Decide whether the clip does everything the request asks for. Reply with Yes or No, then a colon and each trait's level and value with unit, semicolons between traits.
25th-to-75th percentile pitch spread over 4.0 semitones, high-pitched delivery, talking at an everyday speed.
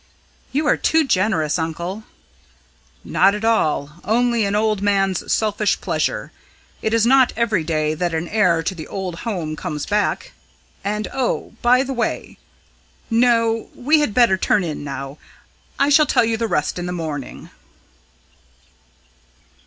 Yes: average, 5.3 semitones; high, 205 Hz; average, 150 wpm